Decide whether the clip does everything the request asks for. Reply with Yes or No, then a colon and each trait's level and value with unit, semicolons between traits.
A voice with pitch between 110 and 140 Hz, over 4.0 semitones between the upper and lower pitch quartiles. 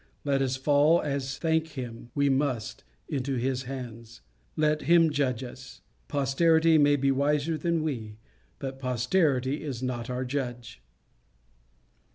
No: low, 135 Hz; average, 3.0 semitones